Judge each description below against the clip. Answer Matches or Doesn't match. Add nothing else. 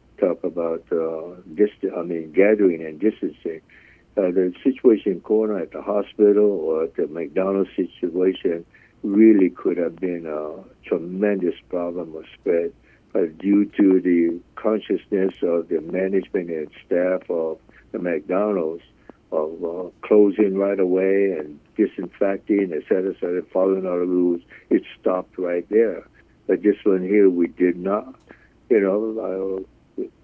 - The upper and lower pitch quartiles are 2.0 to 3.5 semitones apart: Matches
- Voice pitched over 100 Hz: Doesn't match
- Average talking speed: Matches